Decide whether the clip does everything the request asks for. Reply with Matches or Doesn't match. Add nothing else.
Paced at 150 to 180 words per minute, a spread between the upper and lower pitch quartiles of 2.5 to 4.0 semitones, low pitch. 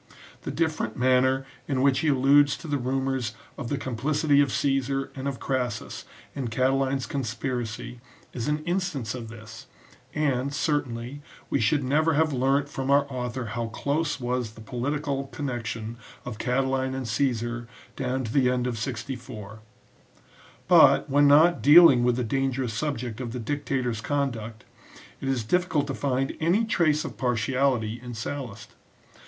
Matches